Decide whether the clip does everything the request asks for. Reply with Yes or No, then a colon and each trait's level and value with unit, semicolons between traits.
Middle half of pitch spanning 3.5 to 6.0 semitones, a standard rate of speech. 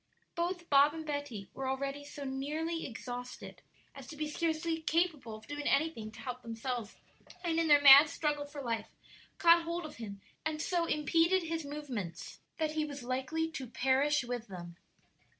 Yes: average, 4.2 semitones; average, 170 wpm